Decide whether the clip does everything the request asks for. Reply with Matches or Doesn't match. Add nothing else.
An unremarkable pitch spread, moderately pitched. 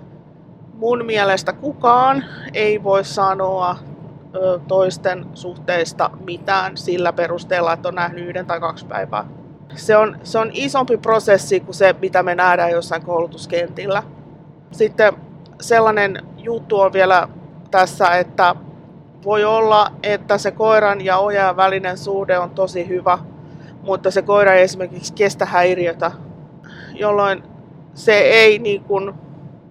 Matches